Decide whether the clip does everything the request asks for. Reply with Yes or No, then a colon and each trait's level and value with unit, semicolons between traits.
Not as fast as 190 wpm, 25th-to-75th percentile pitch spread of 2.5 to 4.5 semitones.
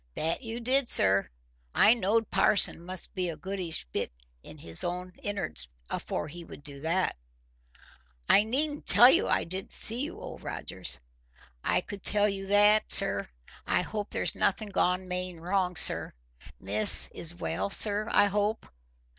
Yes: average, 160 wpm; average, 3.7 semitones